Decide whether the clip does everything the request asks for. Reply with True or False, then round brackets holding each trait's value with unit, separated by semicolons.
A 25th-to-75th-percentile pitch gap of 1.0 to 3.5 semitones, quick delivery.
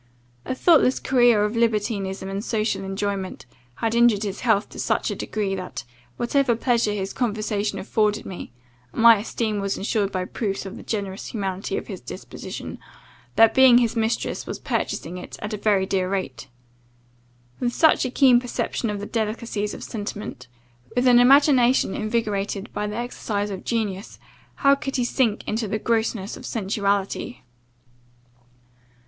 False (3.1 semitones; 160 wpm)